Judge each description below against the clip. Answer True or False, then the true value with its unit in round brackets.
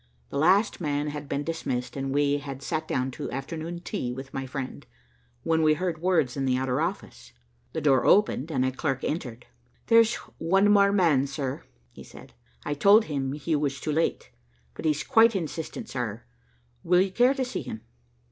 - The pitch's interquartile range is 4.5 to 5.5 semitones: True (4.8 semitones)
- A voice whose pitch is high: False (150 Hz)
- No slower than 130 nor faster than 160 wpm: False (185 wpm)